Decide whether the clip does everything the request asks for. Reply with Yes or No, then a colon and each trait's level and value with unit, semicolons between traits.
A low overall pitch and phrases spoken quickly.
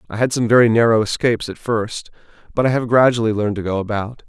Yes: low, 115 Hz; fast, 225 wpm